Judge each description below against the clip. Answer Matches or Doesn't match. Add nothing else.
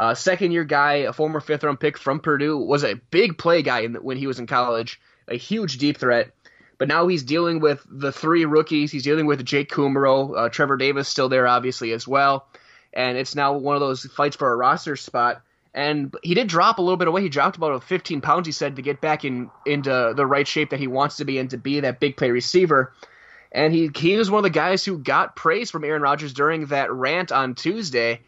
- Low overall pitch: Doesn't match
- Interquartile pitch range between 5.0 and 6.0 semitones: Doesn't match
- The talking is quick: Matches